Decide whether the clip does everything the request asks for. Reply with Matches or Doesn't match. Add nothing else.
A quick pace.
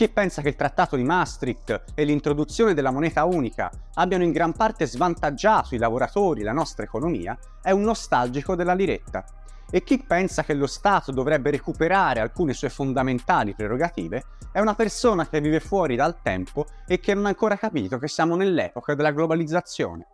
Matches